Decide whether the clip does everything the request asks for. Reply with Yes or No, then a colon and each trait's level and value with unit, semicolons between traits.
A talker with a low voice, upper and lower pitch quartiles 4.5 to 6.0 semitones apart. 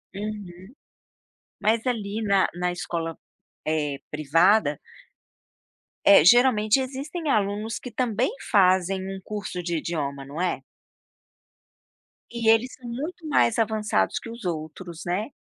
No: high, 200 Hz; average, 4.8 semitones